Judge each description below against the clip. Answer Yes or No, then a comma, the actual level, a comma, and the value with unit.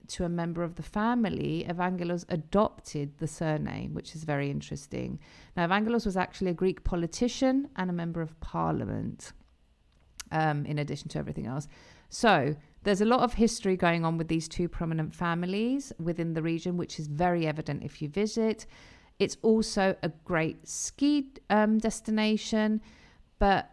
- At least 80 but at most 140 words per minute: No, average, 160 wpm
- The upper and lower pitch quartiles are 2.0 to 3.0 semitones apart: No, average, 5.0 semitones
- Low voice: No, medium, 175 Hz